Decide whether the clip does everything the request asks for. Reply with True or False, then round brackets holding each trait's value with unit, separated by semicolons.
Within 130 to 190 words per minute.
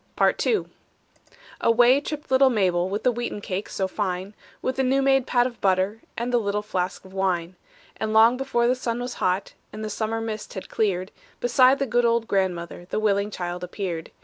False (200 wpm)